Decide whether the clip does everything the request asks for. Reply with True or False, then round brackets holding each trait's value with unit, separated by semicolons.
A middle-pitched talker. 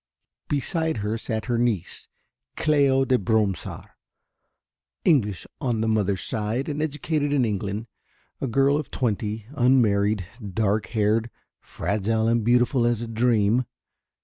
False (115 Hz)